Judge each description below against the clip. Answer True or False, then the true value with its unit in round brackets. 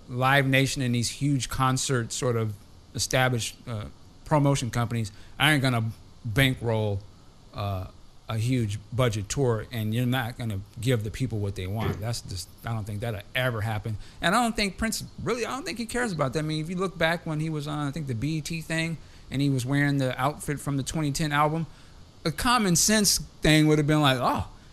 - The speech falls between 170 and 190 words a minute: False (205 wpm)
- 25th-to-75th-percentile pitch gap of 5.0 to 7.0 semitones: True (5.5 semitones)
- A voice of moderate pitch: False (130 Hz)